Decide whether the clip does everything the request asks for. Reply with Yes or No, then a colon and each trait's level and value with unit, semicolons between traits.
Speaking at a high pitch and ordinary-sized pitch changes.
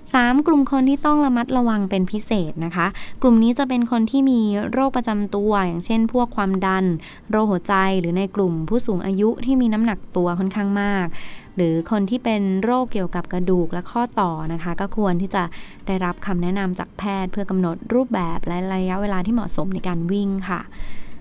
Yes: high, 200 Hz; average, 4.1 semitones